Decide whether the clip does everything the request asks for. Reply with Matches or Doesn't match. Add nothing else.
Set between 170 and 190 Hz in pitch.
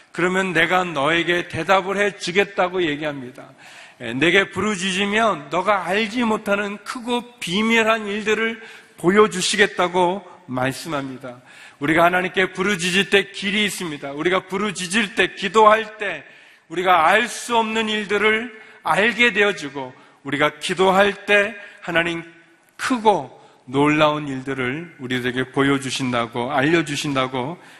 Matches